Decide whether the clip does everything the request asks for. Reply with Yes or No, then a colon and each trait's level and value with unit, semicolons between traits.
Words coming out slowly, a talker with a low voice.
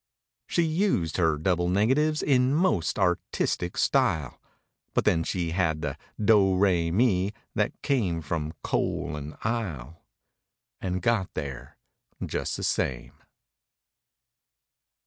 Yes: slow, 115 wpm; very low, 90 Hz